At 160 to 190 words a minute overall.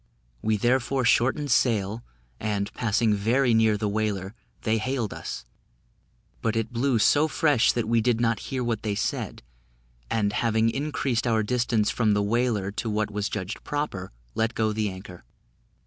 Yes: average, 165 wpm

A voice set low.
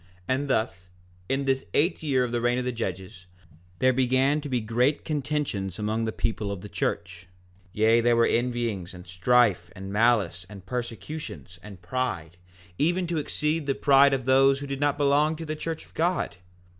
Yes: low, 120 Hz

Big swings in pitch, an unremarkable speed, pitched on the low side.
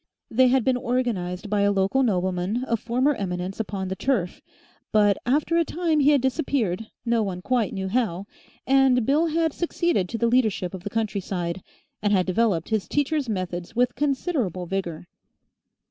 No: wide, 5.7 semitones; average, 170 wpm; high, 225 Hz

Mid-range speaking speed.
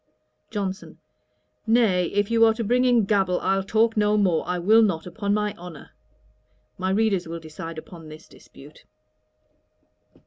Yes: average, 150 wpm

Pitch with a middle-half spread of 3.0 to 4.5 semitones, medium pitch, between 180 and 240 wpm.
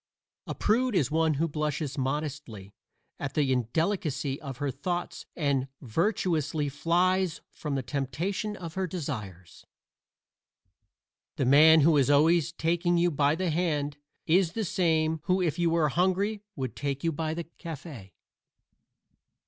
No: average, 3.6 semitones; medium, 155 Hz; average, 140 wpm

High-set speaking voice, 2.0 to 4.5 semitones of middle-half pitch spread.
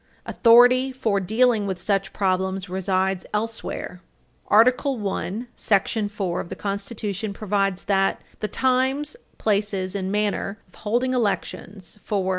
Yes: high, 205 Hz; average, 3.0 semitones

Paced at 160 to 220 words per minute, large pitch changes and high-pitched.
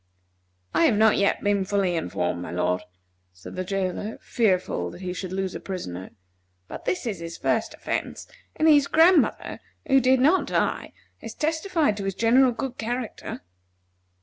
Yes: average, 165 wpm; wide, 6.5 semitones; high, 205 Hz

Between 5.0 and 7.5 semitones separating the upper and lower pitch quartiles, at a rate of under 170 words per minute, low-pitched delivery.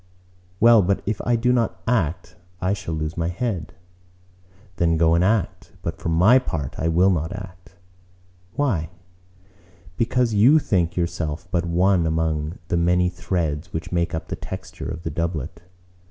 No: average, 3.5 semitones; average, 160 wpm; very low, 85 Hz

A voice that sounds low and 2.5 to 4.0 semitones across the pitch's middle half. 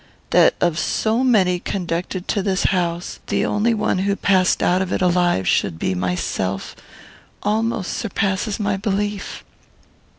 No: high, 190 Hz; average, 2.9 semitones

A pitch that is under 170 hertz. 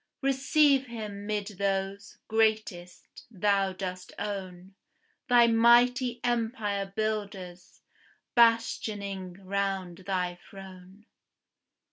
No: high, 200 Hz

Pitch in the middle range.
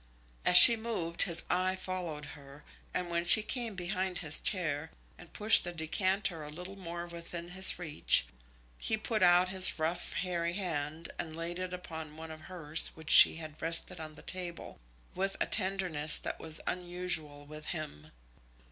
Yes: medium, 175 Hz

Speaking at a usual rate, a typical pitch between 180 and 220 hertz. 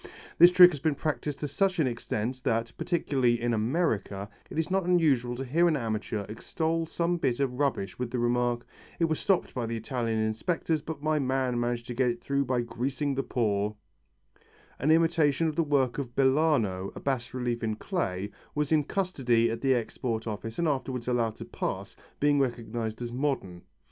No: average, 195 wpm; low, 130 Hz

